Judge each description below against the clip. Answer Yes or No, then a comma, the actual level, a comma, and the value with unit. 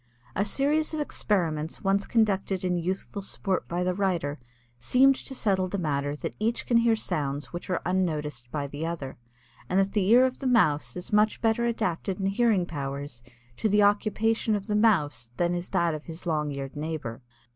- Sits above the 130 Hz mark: Yes, medium, 185 Hz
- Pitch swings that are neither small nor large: No, wide, 5.9 semitones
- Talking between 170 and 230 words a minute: Yes, average, 190 wpm